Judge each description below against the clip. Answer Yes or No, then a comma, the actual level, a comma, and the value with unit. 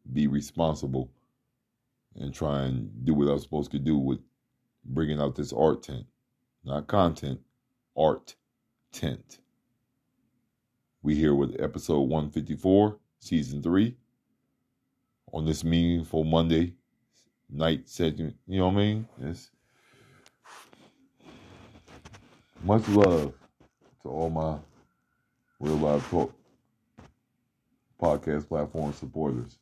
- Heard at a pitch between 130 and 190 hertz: No, very low, 80 Hz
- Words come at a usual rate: No, slow, 105 wpm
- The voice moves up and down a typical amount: Yes, average, 3.9 semitones